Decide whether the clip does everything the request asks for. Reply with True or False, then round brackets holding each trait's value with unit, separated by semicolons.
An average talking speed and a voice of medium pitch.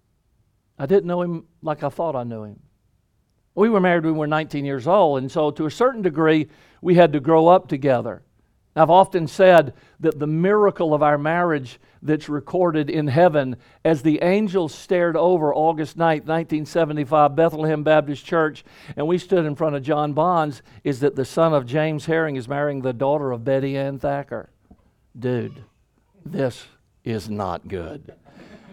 True (175 wpm; 155 Hz)